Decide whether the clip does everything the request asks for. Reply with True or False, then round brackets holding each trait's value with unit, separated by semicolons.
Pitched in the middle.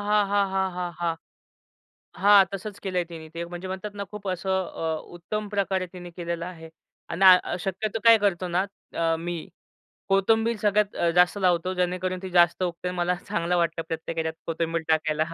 True (180 Hz)